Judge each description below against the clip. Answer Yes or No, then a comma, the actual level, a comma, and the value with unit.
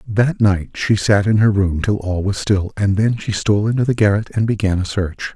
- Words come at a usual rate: No, fast, 245 wpm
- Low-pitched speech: Yes, low, 105 Hz